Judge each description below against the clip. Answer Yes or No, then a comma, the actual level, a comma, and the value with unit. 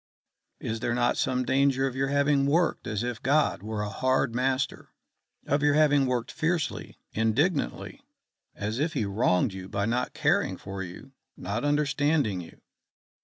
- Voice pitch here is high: No, low, 130 Hz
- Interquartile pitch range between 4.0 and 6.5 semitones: Yes, average, 4.8 semitones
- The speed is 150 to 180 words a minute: Yes, average, 160 wpm